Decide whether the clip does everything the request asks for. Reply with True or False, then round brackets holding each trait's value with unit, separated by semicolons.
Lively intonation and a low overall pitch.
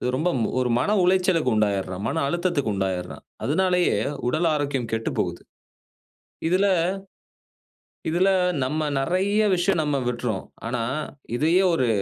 False (6.7 semitones; 150 Hz)